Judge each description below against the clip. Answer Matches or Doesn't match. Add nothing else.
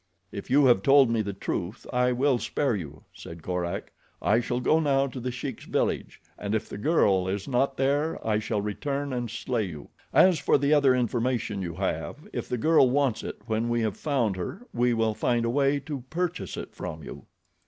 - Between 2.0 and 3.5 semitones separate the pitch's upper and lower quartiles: Doesn't match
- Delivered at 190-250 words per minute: Matches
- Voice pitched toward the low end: Matches